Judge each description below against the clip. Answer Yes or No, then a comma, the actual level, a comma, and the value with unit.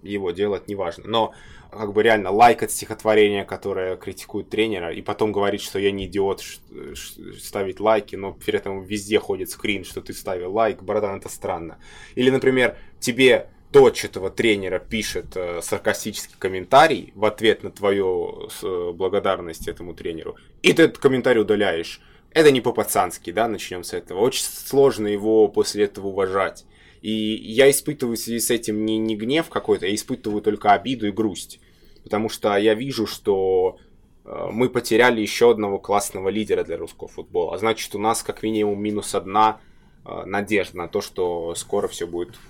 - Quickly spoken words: Yes, fast, 175 wpm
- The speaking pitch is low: Yes, low, 110 Hz